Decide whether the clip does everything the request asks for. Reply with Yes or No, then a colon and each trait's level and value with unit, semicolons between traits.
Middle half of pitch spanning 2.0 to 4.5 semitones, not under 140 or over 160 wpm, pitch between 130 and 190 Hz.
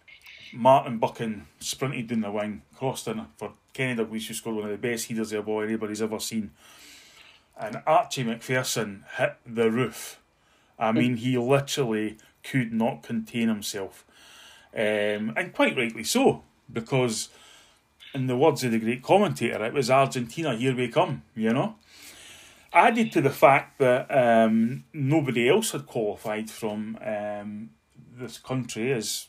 No: average, 3.0 semitones; average, 150 wpm; low, 115 Hz